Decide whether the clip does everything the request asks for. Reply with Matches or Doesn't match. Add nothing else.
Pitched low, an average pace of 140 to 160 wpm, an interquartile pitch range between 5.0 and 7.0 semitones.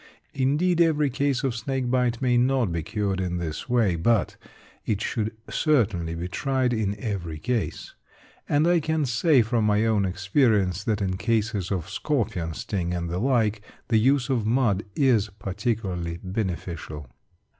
Matches